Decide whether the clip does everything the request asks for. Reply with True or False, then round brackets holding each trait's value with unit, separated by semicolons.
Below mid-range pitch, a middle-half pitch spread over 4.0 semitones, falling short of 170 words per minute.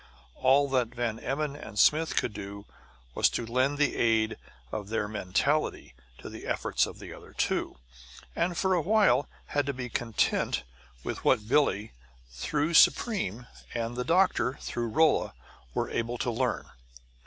True (125 Hz; 4.9 semitones; 155 wpm)